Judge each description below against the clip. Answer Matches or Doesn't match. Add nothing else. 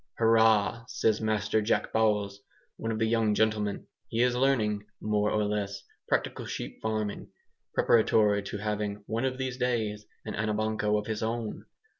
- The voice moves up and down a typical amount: Doesn't match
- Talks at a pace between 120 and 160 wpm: Matches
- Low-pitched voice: Matches